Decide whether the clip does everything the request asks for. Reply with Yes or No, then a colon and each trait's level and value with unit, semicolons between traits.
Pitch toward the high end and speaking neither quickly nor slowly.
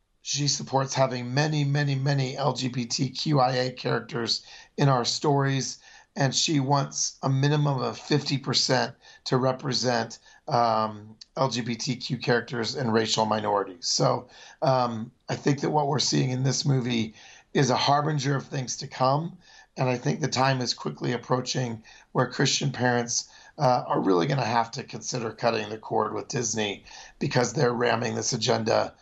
No: low, 125 Hz; average, 150 wpm